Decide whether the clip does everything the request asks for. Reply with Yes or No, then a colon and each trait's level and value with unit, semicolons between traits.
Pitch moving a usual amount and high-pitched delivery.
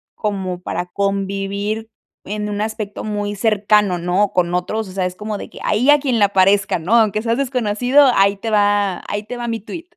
No: narrow, 2.1 semitones; high, 205 Hz